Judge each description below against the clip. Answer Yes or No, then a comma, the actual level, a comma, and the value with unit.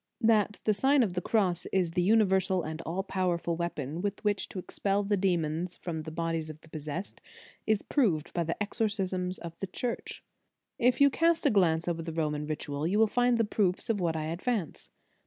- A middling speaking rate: No, fast, 210 wpm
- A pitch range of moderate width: Yes, average, 4.1 semitones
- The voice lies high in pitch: No, medium, 180 Hz